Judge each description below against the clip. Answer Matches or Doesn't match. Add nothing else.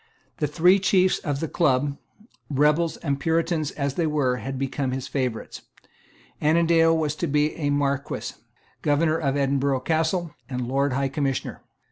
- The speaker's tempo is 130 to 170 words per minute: Matches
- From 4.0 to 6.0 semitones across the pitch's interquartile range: Doesn't match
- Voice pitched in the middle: Matches